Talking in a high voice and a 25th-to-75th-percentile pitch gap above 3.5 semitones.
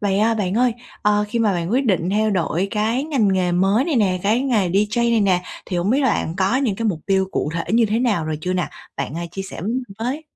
Yes: high, 205 Hz; average, 4.1 semitones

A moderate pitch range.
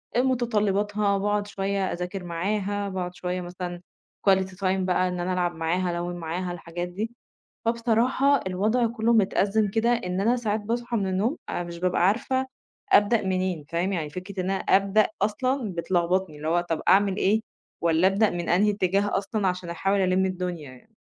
Yes: average, 3.0 semitones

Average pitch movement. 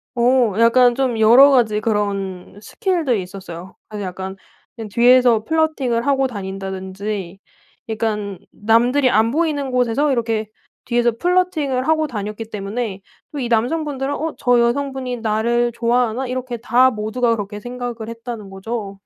Yes: average, 3.5 semitones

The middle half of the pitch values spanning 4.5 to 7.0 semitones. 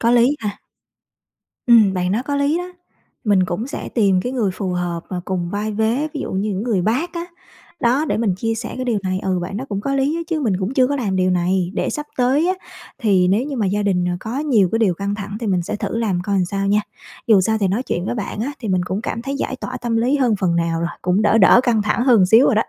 Yes: average, 4.8 semitones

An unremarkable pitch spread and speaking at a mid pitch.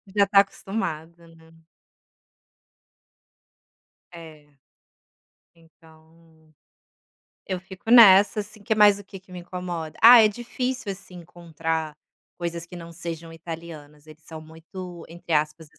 Yes: average, 3.2 semitones; medium, 170 Hz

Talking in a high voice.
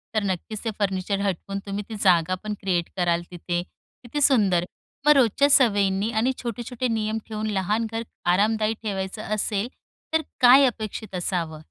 Yes: high, 210 Hz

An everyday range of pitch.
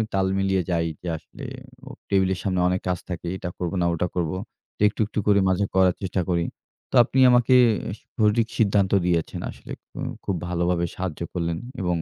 No: narrow, 2.2 semitones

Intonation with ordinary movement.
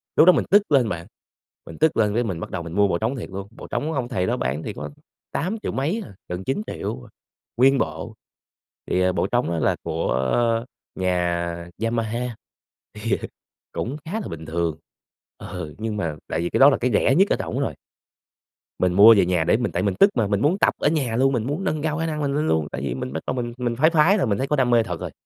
No: wide, 7.7 semitones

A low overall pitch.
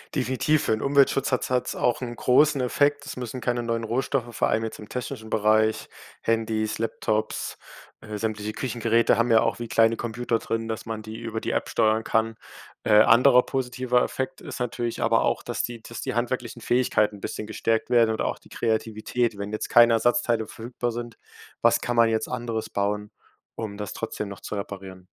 Yes: low, 115 Hz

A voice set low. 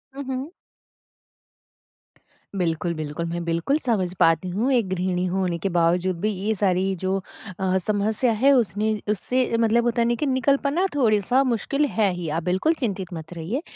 No: high, 200 Hz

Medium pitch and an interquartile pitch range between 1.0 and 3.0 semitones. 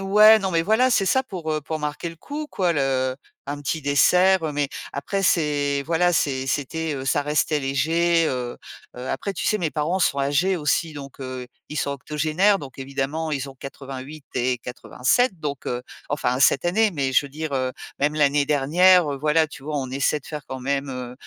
No: medium, 150 Hz; average, 3.7 semitones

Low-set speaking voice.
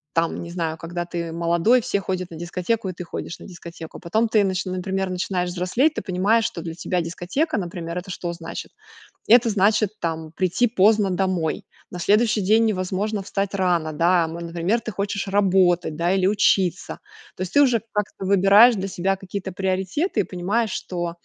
No: medium, 185 Hz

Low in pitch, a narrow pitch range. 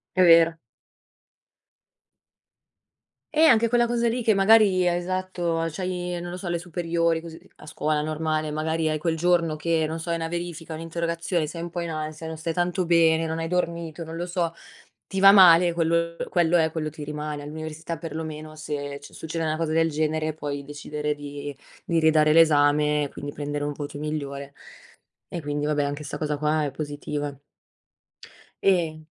No: medium, 160 Hz; narrow, 2.2 semitones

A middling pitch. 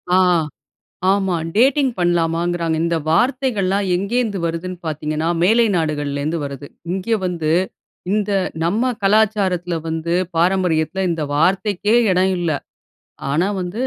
Yes: medium, 180 Hz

